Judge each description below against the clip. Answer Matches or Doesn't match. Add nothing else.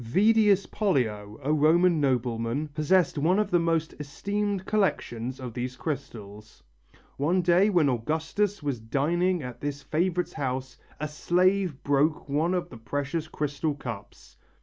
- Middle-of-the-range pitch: Matches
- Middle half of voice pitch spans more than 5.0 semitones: Matches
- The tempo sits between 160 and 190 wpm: Doesn't match